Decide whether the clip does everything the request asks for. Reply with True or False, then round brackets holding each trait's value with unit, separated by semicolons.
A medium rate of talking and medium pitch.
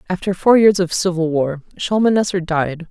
True (165 wpm; 180 Hz)